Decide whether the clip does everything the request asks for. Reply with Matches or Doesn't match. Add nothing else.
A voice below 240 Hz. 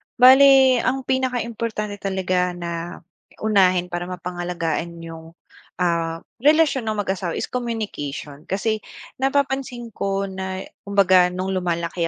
Matches